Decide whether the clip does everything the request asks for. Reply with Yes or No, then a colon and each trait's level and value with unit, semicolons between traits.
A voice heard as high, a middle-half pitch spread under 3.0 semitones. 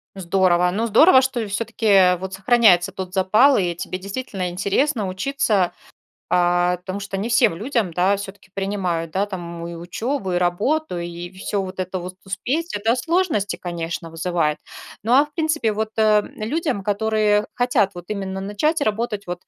No: high, 195 Hz; average, 4.0 semitones